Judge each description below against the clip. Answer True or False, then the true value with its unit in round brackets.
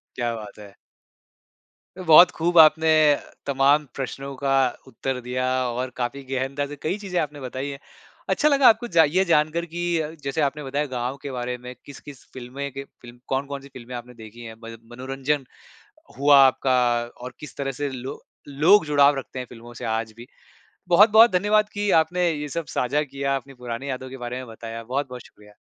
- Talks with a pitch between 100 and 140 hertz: True (135 Hz)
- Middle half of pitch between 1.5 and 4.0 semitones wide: True (3.4 semitones)